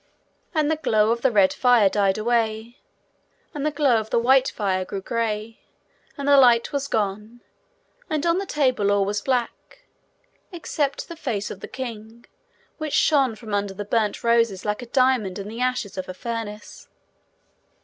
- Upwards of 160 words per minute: Yes, average, 175 wpm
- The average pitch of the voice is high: Yes, high, 230 Hz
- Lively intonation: No, average, 4.1 semitones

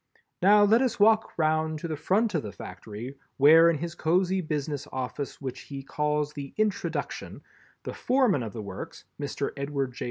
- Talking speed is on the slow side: No, average, 180 wpm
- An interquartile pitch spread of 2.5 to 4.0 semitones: No, average, 5.2 semitones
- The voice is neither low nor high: Yes, medium, 150 Hz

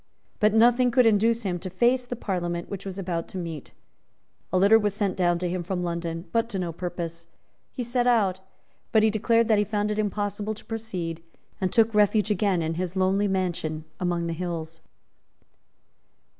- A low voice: No, high, 195 Hz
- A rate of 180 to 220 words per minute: Yes, average, 185 wpm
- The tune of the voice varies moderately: Yes, average, 3.9 semitones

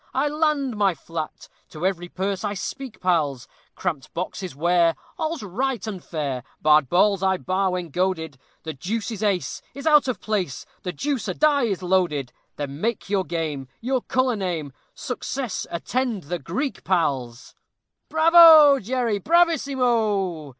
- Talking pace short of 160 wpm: Yes, average, 150 wpm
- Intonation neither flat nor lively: No, wide, 7.2 semitones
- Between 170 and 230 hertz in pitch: Yes, high, 190 Hz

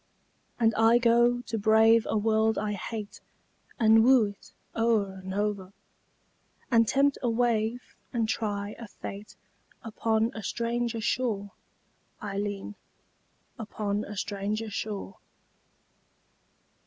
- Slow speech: Yes, slow, 115 wpm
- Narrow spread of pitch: Yes, narrow, 2.1 semitones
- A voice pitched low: No, high, 220 Hz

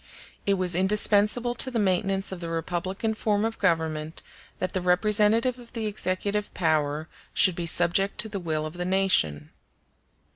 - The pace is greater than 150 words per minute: Yes, average, 160 wpm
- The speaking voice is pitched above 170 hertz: Yes, high, 190 Hz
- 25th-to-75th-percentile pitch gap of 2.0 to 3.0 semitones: No, average, 3.8 semitones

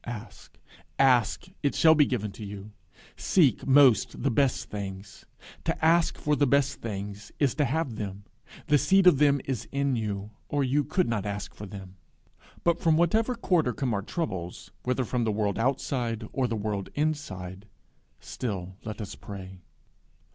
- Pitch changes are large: Yes, wide, 6.0 semitones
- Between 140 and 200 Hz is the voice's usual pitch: No, low, 120 Hz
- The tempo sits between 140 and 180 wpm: Yes, average, 165 wpm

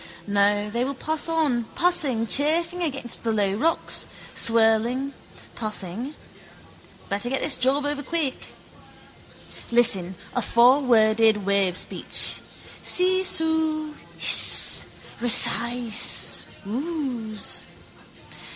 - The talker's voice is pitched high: Yes, high, 245 Hz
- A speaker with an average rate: No, slow, 85 wpm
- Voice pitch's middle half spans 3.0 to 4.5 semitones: No, wide, 5.6 semitones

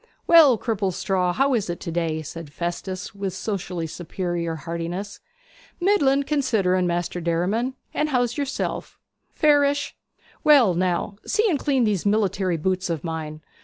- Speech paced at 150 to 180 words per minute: No, slow, 135 wpm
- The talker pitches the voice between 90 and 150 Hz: No, high, 190 Hz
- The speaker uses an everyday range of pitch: No, wide, 7.1 semitones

